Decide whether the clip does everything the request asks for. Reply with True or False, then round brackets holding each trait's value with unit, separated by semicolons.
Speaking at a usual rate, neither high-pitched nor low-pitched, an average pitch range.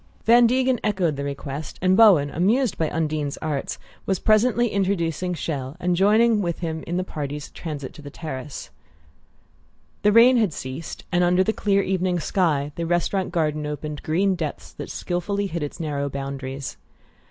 True (165 wpm; 170 Hz; 5.0 semitones)